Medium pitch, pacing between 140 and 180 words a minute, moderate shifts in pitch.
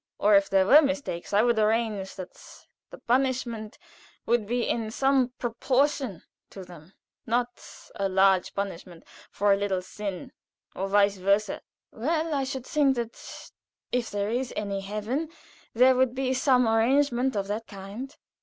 No: high, 225 Hz; average, 155 wpm; average, 4.6 semitones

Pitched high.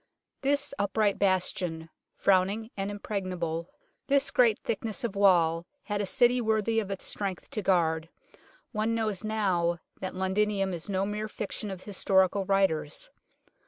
Yes: high, 200 Hz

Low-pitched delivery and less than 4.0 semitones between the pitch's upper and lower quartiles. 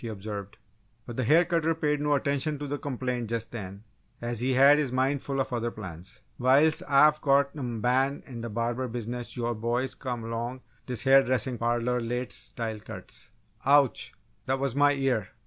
Yes: low, 125 Hz; average, 3.0 semitones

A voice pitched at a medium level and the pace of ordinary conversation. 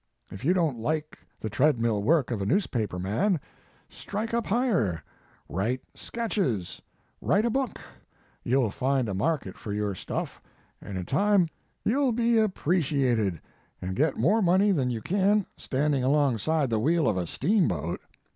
Yes: medium, 145 Hz; average, 165 wpm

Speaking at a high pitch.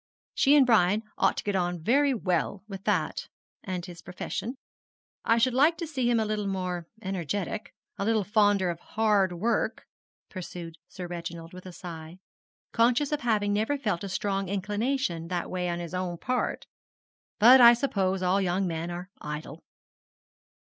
Yes: high, 195 Hz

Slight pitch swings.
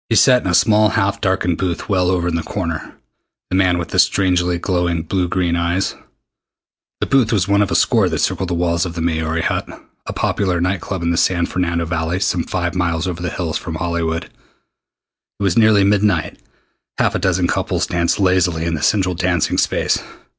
Yes: narrow, 2.0 semitones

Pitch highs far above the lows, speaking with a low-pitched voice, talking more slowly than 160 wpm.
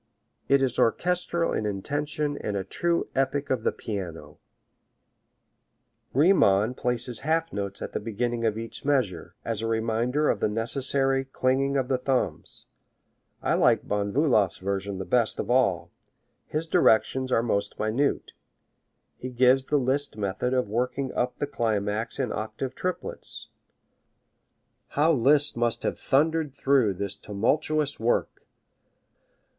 No: average, 4.4 semitones; low, 125 Hz; average, 140 wpm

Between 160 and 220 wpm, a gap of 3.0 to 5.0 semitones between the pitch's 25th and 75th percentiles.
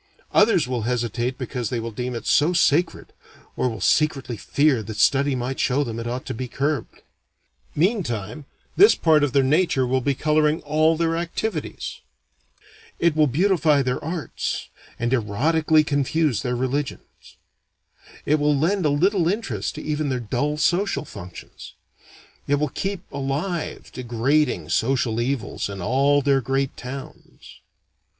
No: average, 150 wpm; average, 3.9 semitones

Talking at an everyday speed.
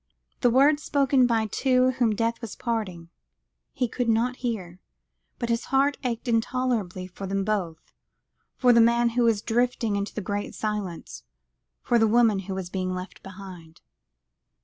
Yes: average, 165 wpm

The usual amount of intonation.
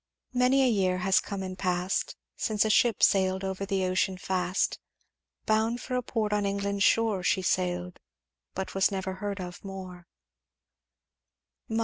No: narrow, 2.1 semitones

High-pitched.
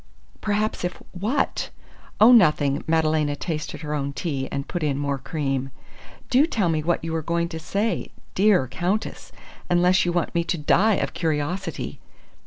No: medium, 165 Hz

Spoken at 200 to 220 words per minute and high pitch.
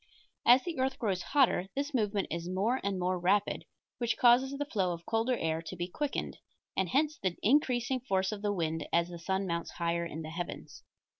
Yes: fast, 205 wpm; high, 195 Hz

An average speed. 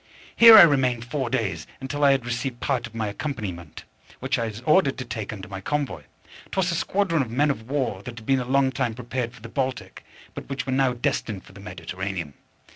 No: fast, 220 wpm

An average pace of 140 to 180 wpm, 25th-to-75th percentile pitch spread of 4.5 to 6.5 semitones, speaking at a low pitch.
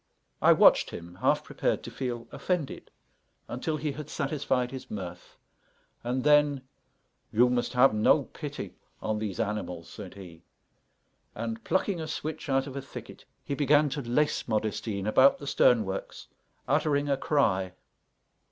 Yes: average, 150 wpm; average, 5.2 semitones; low, 125 Hz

